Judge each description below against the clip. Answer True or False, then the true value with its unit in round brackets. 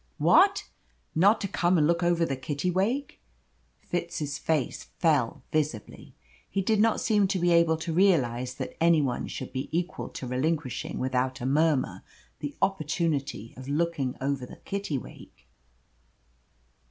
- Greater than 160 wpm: False (140 wpm)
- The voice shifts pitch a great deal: False (4.7 semitones)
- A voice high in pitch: False (160 Hz)